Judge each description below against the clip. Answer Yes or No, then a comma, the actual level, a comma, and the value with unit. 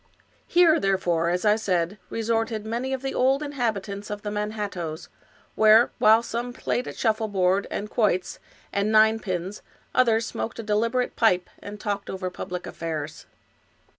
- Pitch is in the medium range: No, high, 210 Hz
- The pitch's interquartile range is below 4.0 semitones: Yes, average, 3.2 semitones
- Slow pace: No, average, 155 wpm